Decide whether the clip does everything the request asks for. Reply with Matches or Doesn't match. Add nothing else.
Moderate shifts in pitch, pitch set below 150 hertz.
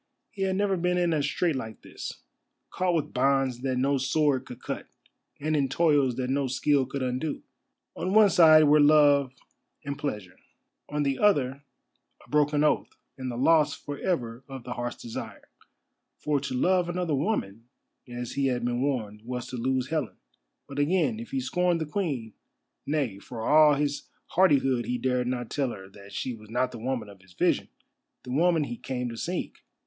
Matches